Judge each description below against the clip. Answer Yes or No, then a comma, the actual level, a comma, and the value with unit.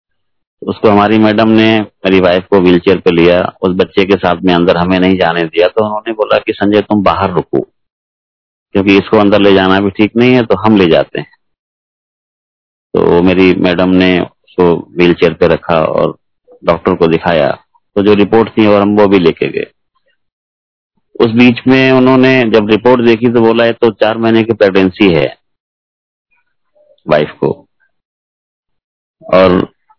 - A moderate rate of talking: Yes, average, 165 wpm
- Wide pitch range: No, average, 4.0 semitones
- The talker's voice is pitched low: Yes, low, 105 Hz